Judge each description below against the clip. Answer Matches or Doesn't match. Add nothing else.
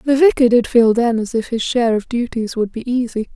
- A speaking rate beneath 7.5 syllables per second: Matches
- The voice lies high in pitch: Matches